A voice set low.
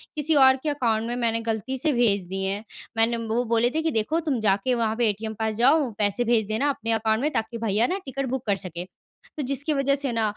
No: high, 235 Hz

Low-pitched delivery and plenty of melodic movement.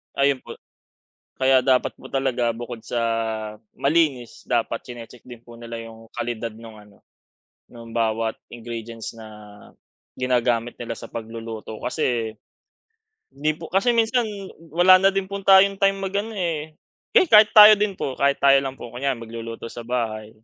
Yes: low, 125 Hz; wide, 5.8 semitones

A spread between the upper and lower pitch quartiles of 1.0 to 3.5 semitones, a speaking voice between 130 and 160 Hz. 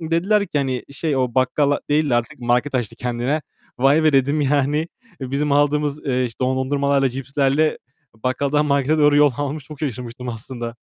Yes: narrow, 2.5 semitones; medium, 140 Hz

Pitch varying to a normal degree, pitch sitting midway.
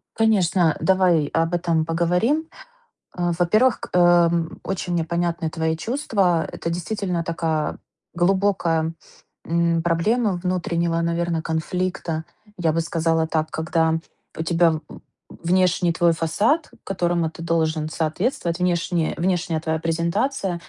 No: narrow, 1.8 semitones; medium, 170 Hz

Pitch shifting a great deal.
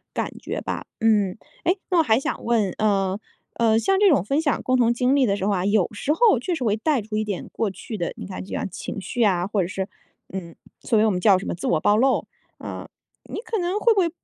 Yes: wide, 5.8 semitones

